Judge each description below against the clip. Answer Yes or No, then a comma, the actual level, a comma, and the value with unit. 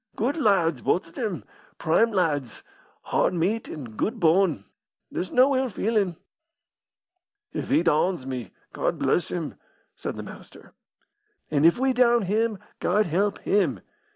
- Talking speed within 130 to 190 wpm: Yes, average, 145 wpm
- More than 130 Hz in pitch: Yes, high, 190 Hz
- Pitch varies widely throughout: Yes, wide, 5.9 semitones